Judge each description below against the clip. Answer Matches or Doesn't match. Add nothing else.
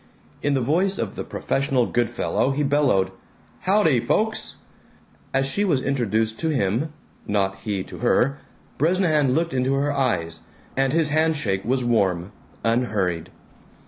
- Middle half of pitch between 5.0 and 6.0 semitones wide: Matches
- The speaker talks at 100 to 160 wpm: Matches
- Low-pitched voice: Matches